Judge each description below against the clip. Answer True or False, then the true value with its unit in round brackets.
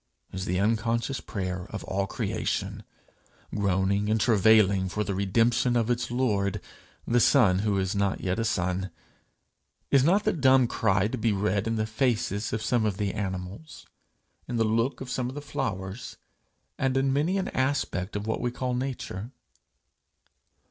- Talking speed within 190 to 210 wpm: False (170 wpm)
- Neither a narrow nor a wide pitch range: True (4.1 semitones)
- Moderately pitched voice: False (110 Hz)